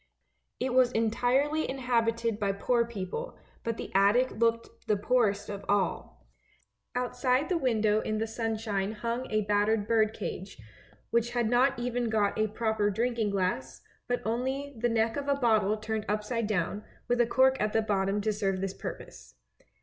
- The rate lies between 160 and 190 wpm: Yes, average, 165 wpm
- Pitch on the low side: No, high, 225 Hz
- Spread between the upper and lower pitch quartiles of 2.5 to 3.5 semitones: Yes, average, 2.8 semitones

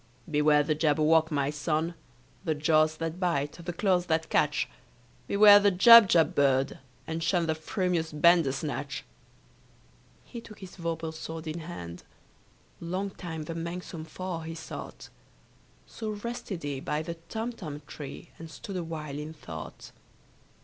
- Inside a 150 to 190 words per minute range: No, average, 140 wpm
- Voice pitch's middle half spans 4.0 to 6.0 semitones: No, average, 2.8 semitones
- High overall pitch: No, medium, 160 Hz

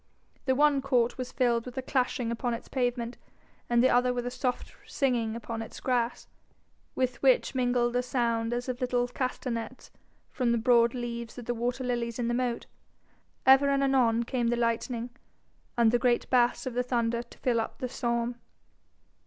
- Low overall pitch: No, high, 245 Hz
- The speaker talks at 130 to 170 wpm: No, average, 185 wpm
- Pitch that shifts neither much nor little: No, narrow, 1.3 semitones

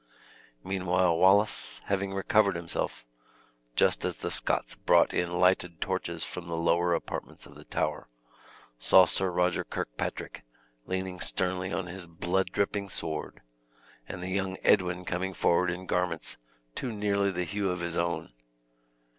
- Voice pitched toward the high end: No, very low, 90 Hz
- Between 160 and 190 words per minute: No, average, 145 wpm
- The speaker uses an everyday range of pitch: No, narrow, 1.7 semitones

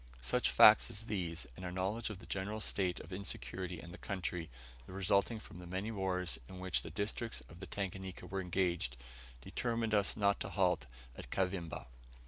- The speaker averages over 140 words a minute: Yes, average, 180 wpm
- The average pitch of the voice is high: No, very low, 95 Hz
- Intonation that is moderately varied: No, narrow, 2.3 semitones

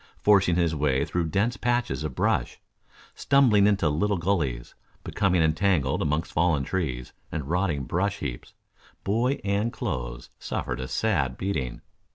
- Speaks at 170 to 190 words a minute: No, average, 140 wpm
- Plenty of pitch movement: Yes, wide, 5.7 semitones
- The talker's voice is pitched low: Yes, very low, 85 Hz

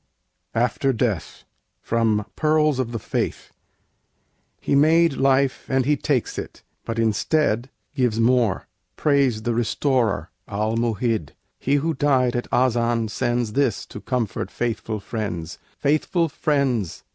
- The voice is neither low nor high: No, low, 120 Hz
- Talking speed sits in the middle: No, slow, 125 wpm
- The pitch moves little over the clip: No, average, 3.8 semitones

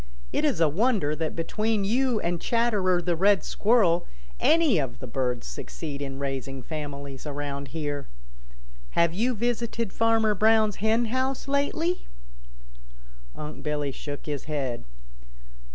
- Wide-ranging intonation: Yes, wide, 7.8 semitones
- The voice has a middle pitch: Yes, medium, 170 Hz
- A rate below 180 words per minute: Yes, slow, 135 wpm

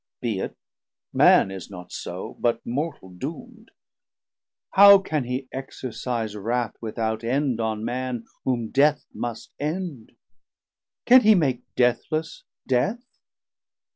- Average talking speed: No, slow, 115 wpm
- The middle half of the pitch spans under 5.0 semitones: No, wide, 5.4 semitones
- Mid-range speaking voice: No, low, 125 Hz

